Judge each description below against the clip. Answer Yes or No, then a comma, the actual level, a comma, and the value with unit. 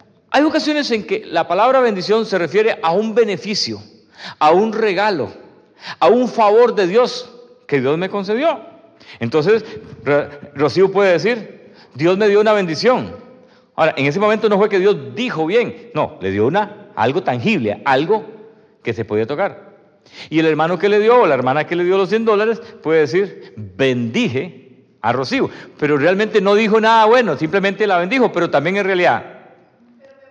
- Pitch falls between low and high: No, high, 205 Hz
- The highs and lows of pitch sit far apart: Yes, wide, 5.8 semitones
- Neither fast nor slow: Yes, average, 170 wpm